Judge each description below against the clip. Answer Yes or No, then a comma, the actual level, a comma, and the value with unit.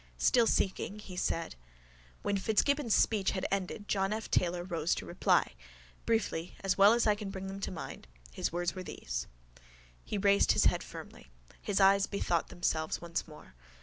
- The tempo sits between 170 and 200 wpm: Yes, average, 175 wpm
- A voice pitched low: No, high, 195 Hz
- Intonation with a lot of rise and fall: No, average, 2.8 semitones